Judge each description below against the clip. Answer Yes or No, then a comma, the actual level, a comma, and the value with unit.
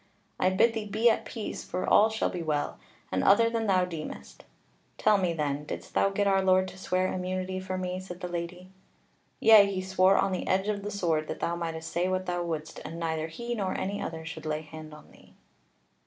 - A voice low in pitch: No, medium, 185 Hz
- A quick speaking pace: Yes, fast, 220 wpm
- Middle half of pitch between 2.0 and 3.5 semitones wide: Yes, average, 3.1 semitones